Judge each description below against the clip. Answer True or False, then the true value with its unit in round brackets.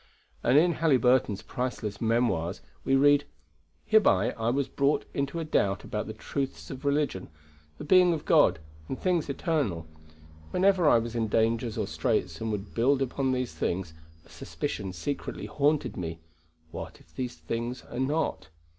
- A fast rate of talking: False (160 wpm)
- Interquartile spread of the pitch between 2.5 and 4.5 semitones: False (4.9 semitones)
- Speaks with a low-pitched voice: True (130 Hz)